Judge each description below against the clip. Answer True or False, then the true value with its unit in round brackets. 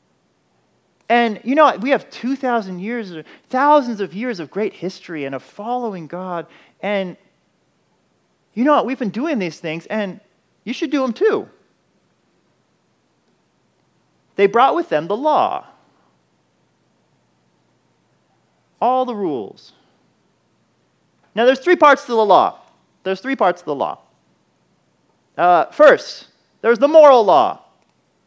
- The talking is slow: True (130 wpm)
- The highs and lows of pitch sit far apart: True (6.2 semitones)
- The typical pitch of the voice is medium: False (230 Hz)